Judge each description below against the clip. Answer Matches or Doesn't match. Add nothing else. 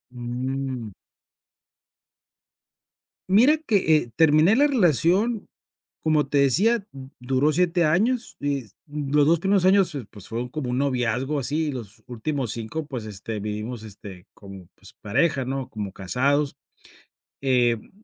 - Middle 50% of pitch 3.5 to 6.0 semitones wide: Matches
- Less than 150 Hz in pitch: Matches